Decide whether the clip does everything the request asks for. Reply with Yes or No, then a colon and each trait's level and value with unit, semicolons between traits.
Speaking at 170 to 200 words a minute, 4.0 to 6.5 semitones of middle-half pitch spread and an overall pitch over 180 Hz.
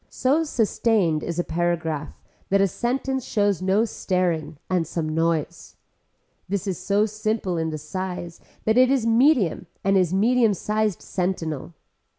No: average, 145 wpm; average, 4.6 semitones; high, 190 Hz